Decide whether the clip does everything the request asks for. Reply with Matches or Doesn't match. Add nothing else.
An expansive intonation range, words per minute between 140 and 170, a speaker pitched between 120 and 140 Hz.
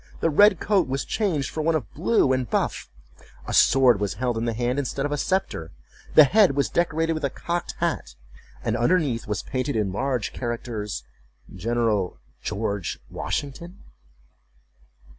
Matches